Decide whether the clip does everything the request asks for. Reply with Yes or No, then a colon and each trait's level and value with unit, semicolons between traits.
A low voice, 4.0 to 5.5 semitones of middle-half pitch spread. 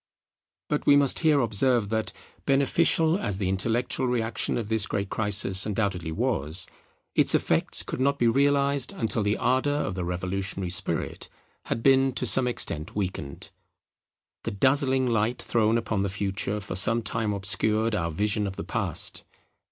Yes: low, 110 Hz; average, 4.9 semitones